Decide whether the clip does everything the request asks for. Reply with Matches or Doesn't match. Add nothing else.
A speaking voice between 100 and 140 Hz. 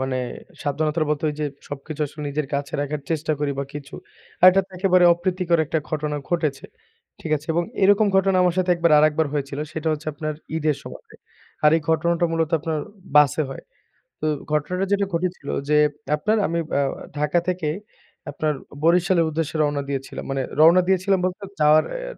Doesn't match